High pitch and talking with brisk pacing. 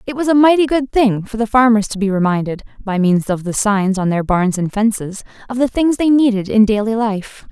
Yes: high, 220 Hz; fast, 240 wpm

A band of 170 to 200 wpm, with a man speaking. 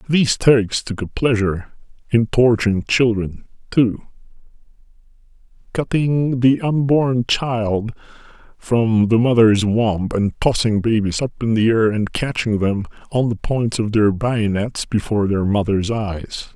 No: slow, 135 wpm; male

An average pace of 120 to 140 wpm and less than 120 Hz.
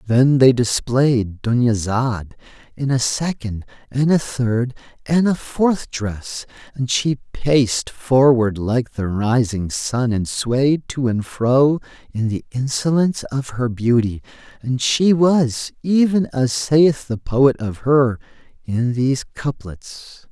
No: slow, 135 wpm; low, 125 Hz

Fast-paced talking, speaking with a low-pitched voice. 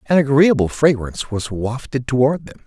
No: average, 155 wpm; low, 130 Hz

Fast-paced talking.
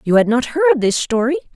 Yes: fast, 230 wpm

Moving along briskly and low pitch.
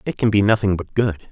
Yes: fast, 275 wpm; low, 105 Hz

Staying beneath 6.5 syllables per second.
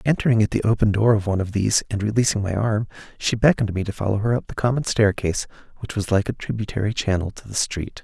No: 6.8 syllables/s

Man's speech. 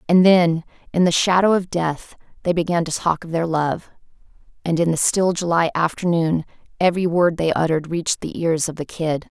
No: female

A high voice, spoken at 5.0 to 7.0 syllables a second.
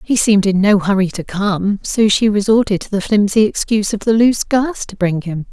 Yes: high, 205 Hz; 5.4 syllables/s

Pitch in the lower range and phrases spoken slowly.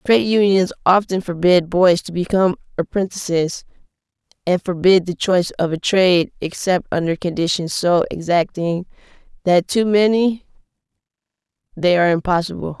No: medium, 180 Hz; slow, 120 wpm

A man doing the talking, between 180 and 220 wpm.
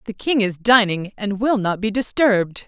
No: female; average, 200 wpm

